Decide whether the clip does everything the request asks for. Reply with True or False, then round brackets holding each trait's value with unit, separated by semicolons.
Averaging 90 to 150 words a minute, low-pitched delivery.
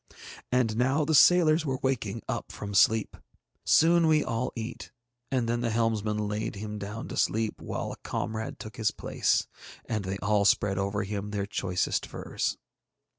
False (170 wpm; 110 Hz)